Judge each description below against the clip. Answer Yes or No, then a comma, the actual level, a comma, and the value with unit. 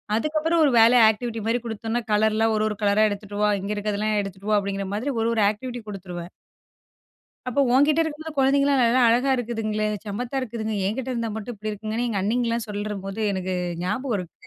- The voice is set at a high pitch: Yes, high, 220 Hz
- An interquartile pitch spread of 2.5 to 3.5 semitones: Yes, average, 3.0 semitones